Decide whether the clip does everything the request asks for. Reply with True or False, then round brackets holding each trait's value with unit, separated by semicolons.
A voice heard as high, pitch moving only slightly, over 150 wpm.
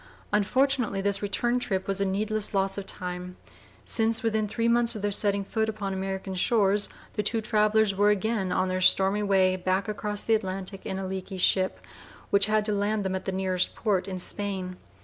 True (200 Hz; 2.1 semitones; 195 wpm)